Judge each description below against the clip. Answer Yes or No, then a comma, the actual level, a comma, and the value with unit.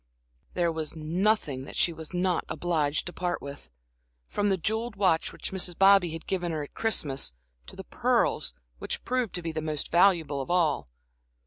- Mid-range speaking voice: Yes, medium, 170 Hz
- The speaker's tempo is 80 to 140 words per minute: No, average, 185 wpm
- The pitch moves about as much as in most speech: Yes, average, 3.7 semitones